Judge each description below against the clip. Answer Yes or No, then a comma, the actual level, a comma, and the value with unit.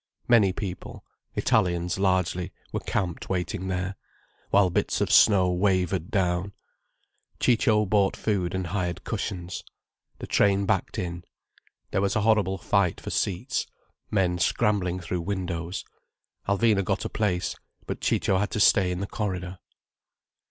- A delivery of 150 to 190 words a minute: No, slow, 135 wpm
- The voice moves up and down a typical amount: No, narrow, 2.1 semitones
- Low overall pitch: Yes, very low, 95 Hz